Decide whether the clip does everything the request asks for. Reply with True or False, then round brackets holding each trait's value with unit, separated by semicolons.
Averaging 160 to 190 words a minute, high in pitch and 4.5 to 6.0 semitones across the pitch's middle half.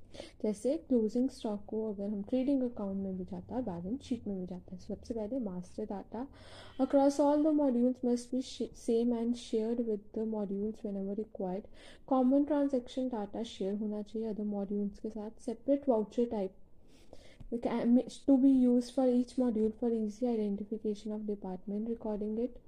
False (165 wpm; 225 Hz; 3.2 semitones)